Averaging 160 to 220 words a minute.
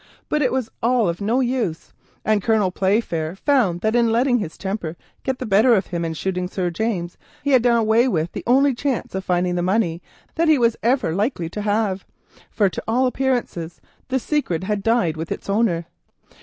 Yes: average, 195 wpm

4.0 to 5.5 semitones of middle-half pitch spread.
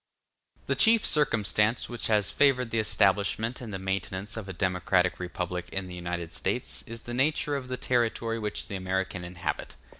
Yes: average, 4.3 semitones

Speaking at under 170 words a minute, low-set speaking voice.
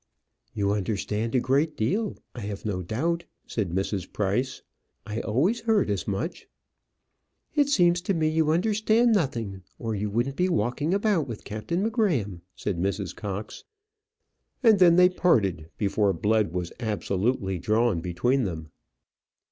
Yes: average, 145 wpm; low, 115 Hz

